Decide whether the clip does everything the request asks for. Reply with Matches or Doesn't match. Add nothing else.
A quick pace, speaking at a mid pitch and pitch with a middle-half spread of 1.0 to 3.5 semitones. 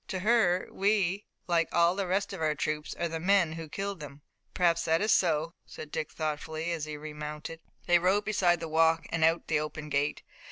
Matches